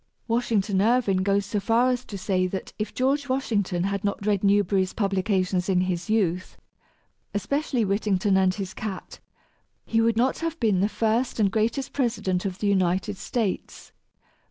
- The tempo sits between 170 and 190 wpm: No, average, 160 wpm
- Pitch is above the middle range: Yes, high, 205 Hz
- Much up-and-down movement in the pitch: No, average, 3.2 semitones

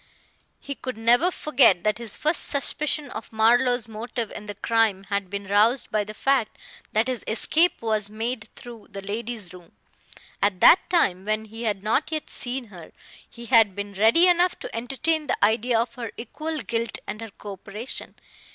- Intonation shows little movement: No, average, 3.5 semitones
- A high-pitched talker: Yes, high, 225 Hz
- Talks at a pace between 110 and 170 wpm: No, average, 180 wpm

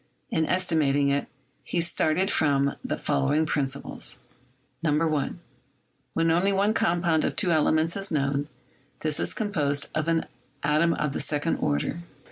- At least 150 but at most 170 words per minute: No, average, 140 wpm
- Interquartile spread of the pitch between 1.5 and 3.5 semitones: Yes, average, 2.8 semitones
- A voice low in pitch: No, medium, 155 Hz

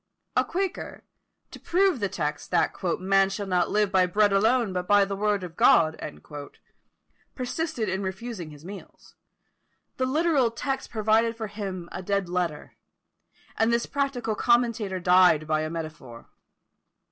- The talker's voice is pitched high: Yes, high, 200 Hz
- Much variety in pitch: No, average, 4.6 semitones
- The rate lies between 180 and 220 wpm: No, average, 145 wpm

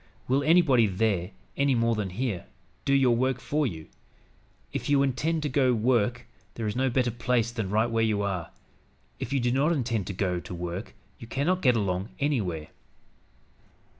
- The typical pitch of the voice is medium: No, low, 120 Hz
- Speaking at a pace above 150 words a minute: Yes, average, 185 wpm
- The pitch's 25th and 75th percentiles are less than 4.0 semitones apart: No, average, 4.7 semitones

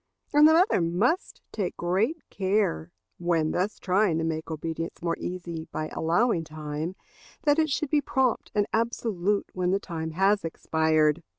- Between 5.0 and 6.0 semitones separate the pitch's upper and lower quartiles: Yes, average, 5.3 semitones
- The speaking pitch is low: No, medium, 180 Hz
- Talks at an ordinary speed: Yes, average, 160 wpm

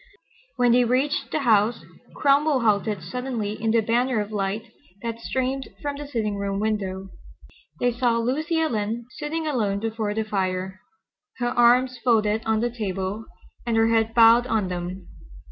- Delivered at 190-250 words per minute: No, average, 160 wpm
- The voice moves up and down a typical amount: Yes, average, 3.2 semitones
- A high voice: Yes, high, 225 Hz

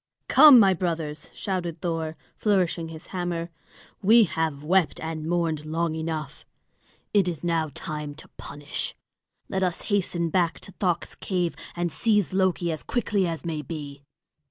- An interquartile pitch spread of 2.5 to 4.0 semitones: Yes, average, 2.9 semitones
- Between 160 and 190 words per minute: No, average, 150 wpm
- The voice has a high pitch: No, medium, 170 Hz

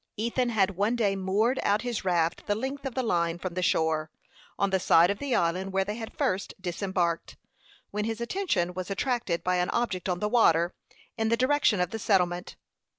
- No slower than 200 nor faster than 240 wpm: Yes, fast, 205 wpm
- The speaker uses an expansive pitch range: No, average, 4.4 semitones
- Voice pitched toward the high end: Yes, high, 195 Hz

